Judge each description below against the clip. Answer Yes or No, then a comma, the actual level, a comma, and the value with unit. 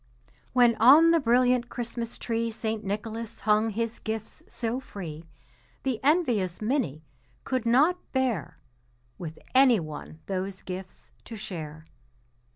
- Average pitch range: Yes, average, 4.6 semitones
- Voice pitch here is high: Yes, high, 225 Hz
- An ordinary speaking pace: No, slow, 125 wpm